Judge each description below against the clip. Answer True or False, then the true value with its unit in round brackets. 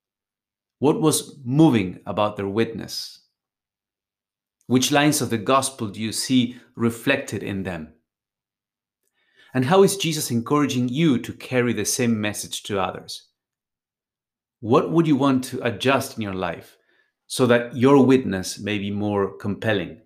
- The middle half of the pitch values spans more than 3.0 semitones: True (5.0 semitones)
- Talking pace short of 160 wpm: True (140 wpm)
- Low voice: True (115 Hz)